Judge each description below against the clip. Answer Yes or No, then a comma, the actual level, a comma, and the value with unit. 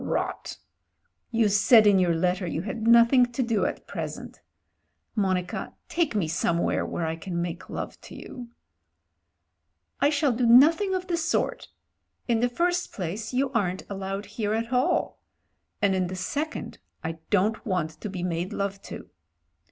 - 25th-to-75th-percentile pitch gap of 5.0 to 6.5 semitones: Yes, average, 5.3 semitones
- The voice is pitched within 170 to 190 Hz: No, high, 210 Hz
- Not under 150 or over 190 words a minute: Yes, average, 160 wpm